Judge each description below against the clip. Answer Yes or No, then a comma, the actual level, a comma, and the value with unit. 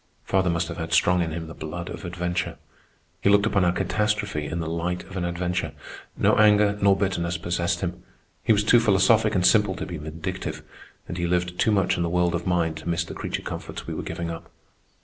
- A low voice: Yes, very low, 90 Hz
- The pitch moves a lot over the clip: No, narrow, 2.4 semitones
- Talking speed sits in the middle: No, fast, 225 wpm